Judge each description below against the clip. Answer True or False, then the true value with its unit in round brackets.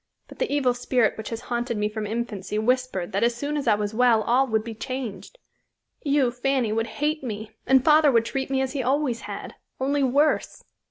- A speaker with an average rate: False (210 wpm)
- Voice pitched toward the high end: True (245 Hz)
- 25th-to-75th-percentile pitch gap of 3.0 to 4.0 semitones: True (3.5 semitones)